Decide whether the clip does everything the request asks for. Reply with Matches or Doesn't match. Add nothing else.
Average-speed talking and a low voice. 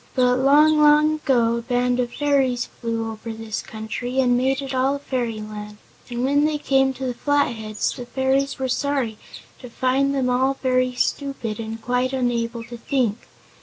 Doesn't match